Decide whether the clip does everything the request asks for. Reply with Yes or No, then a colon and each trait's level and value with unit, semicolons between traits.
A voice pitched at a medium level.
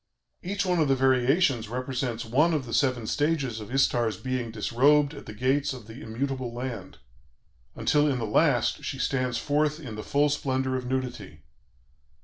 No: low, 130 Hz